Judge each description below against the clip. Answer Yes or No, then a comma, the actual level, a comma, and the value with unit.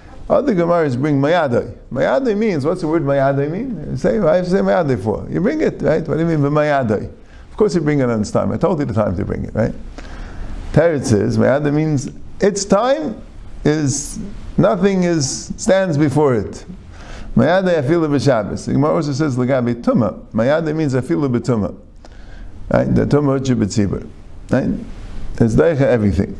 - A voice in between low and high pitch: Yes, medium, 150 Hz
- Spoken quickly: No, average, 175 wpm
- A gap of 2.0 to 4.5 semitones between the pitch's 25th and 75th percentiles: No, average, 5.0 semitones